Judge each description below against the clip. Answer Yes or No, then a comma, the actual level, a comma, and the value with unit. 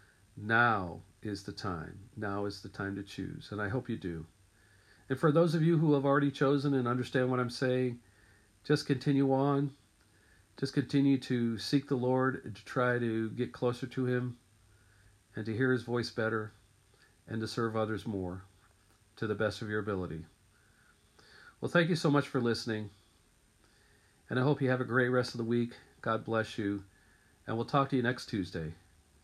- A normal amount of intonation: Yes, average, 4.1 semitones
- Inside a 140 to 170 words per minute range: No, average, 185 wpm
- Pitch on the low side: Yes, low, 110 Hz